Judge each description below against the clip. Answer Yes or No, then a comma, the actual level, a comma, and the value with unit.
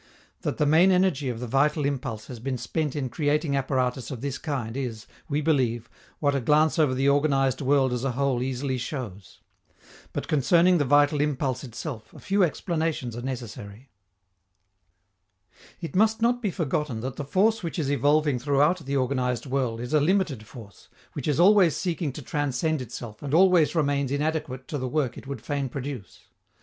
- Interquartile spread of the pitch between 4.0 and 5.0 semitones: No, average, 3.4 semitones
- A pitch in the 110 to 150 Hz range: Yes, medium, 140 Hz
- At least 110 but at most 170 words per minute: No, average, 180 wpm